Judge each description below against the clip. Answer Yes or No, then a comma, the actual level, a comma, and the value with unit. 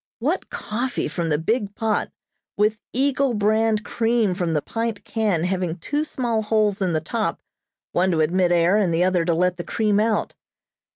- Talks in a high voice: Yes, high, 205 Hz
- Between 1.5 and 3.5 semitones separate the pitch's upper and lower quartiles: No, average, 4.1 semitones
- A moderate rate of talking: Yes, average, 180 wpm